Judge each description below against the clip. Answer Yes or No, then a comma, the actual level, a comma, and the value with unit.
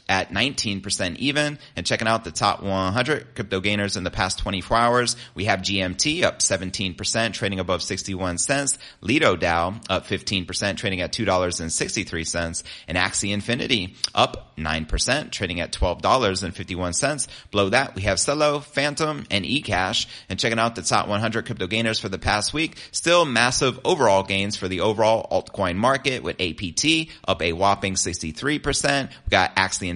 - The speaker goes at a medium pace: Yes, average, 155 wpm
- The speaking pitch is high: No, low, 100 Hz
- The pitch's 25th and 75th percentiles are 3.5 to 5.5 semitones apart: Yes, average, 4.2 semitones